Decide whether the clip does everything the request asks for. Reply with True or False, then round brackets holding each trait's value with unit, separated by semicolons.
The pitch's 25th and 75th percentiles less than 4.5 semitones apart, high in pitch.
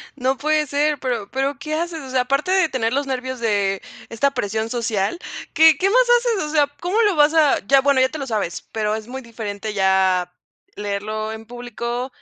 False (5.3 semitones; 255 Hz)